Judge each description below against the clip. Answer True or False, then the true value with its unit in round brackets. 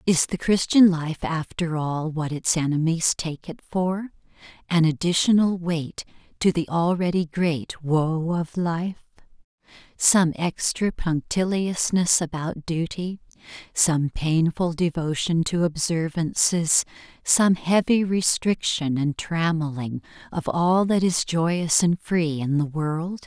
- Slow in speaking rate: True (120 wpm)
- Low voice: False (165 Hz)